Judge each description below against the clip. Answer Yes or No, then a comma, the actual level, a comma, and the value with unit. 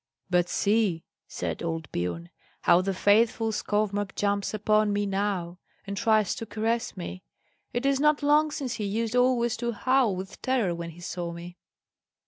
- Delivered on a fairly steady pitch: No, average, 4.3 semitones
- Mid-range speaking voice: No, high, 205 Hz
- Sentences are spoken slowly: No, average, 165 wpm